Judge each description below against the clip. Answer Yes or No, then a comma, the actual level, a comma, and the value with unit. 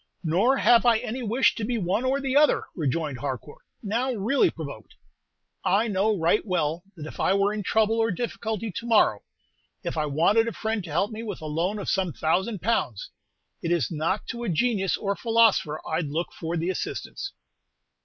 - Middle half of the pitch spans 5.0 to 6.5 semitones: Yes, wide, 5.6 semitones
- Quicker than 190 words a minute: Yes, average, 200 wpm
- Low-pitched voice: No, high, 200 Hz